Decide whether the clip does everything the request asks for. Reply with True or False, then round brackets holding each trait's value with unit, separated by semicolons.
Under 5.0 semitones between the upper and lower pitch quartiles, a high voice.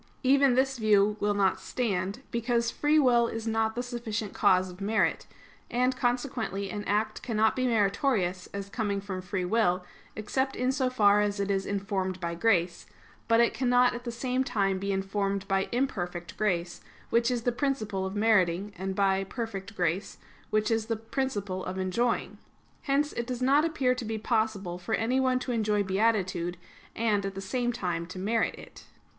True (4.0 semitones; 215 Hz)